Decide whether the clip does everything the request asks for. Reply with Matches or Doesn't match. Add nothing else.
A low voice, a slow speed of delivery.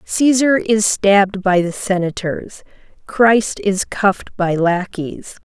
Doesn't match